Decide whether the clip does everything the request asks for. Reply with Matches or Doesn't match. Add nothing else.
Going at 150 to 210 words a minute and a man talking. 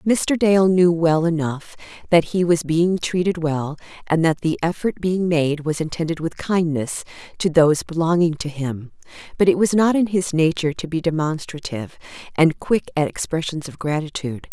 Doesn't match